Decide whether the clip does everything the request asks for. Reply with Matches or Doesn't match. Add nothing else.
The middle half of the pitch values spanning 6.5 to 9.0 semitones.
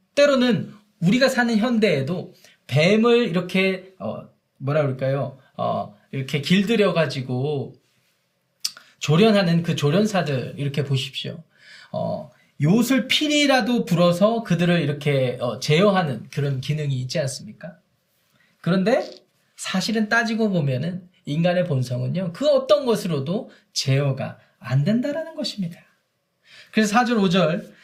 Matches